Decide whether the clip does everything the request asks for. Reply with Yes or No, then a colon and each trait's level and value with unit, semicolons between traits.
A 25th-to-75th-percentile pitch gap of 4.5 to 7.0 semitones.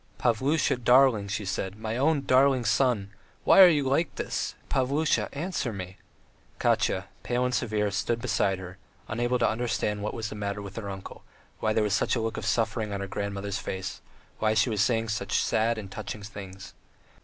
No: average, 3.7 semitones